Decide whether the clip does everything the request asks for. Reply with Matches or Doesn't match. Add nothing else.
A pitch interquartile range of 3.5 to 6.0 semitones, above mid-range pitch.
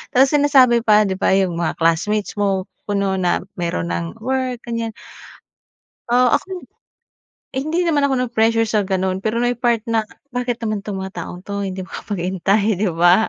Matches